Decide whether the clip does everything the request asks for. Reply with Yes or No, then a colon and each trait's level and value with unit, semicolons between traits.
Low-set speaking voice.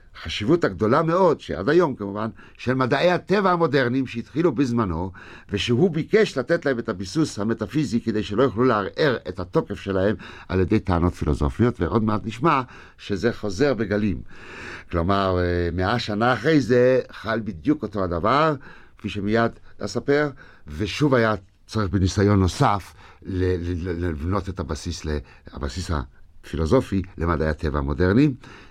Yes: low, 105 Hz